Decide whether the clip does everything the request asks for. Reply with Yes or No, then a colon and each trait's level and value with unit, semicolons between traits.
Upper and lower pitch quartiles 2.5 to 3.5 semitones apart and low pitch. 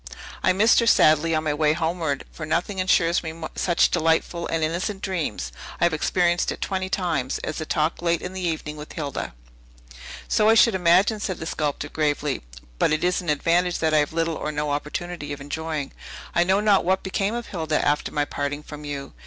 No: average, 3.2 semitones; medium, 165 Hz